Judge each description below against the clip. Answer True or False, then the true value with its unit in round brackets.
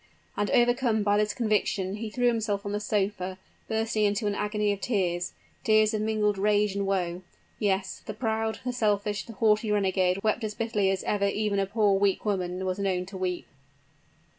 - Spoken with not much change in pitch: True (1.9 semitones)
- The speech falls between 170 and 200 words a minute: True (190 wpm)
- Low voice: False (205 Hz)